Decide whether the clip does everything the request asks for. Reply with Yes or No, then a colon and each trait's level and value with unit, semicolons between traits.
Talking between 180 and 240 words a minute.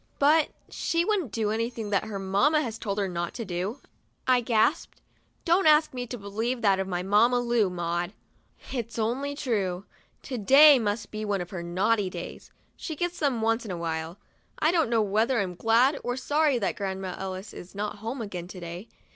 Yes: fast, 205 wpm